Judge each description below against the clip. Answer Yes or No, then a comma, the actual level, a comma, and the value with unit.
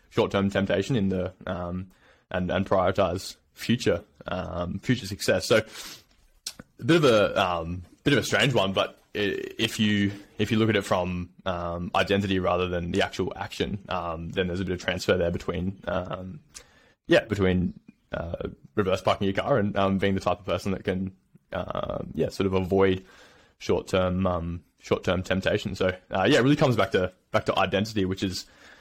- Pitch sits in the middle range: No, very low, 95 Hz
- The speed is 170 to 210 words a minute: Yes, average, 180 wpm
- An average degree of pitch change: No, narrow, 1.6 semitones